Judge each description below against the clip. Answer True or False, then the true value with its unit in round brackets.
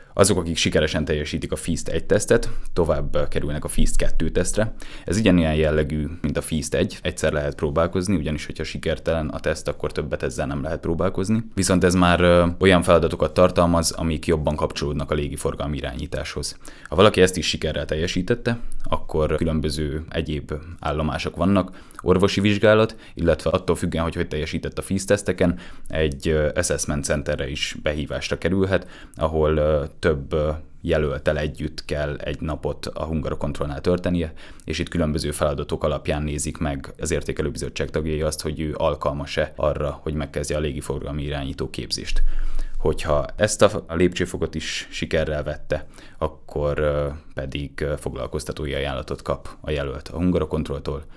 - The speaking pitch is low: True (80 Hz)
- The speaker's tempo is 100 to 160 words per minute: True (140 wpm)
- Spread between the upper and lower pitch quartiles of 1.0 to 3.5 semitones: True (2.9 semitones)